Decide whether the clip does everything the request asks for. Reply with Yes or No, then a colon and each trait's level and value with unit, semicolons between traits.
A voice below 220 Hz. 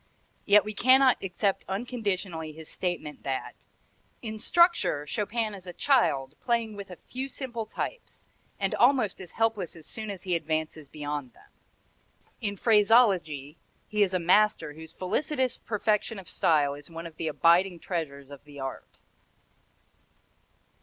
Yes: high, 190 Hz